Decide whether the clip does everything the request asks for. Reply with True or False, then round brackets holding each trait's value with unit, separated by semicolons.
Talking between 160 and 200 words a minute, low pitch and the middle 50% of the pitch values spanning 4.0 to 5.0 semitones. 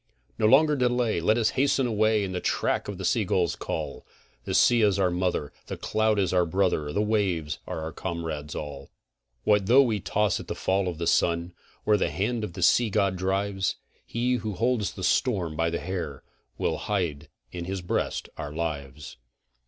True (195 wpm; 95 Hz; 4.3 semitones)